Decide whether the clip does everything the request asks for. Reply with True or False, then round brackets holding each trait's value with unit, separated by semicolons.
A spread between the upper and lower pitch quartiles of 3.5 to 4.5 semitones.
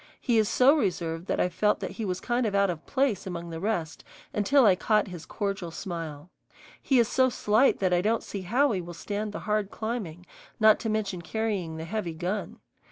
True (4.0 semitones)